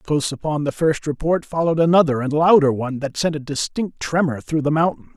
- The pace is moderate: No, fast, 210 wpm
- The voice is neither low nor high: Yes, medium, 150 Hz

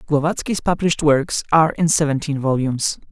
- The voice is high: No, medium, 150 Hz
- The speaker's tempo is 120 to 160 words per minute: Yes, slow, 135 wpm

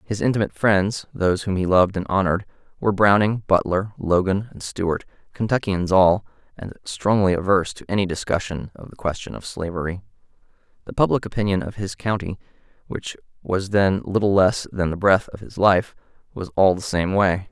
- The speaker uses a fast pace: No, average, 170 wpm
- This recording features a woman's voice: No, male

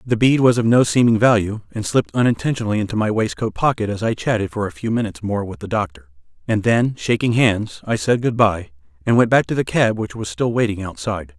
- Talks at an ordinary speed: No, fast, 225 wpm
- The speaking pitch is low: Yes, low, 110 Hz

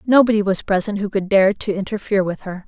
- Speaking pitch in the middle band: No, high, 200 Hz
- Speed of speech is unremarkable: No, fast, 225 wpm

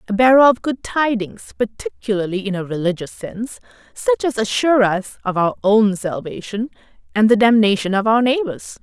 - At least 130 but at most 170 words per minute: Yes, average, 165 wpm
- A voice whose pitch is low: No, high, 220 Hz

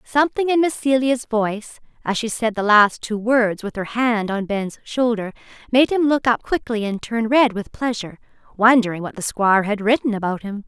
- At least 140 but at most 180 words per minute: No, average, 200 wpm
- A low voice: No, high, 225 Hz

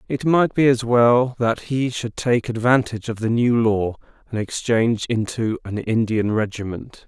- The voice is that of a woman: No, male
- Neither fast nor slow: Yes, average, 170 wpm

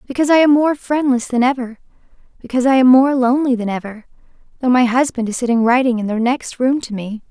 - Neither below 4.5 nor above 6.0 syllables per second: No, 6.4 syllables/s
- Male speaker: No, female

